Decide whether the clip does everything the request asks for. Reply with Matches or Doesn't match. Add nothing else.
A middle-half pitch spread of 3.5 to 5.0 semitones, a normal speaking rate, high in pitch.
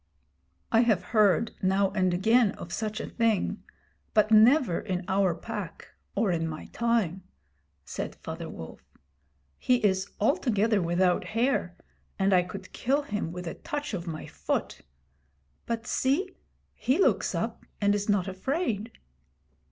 Matches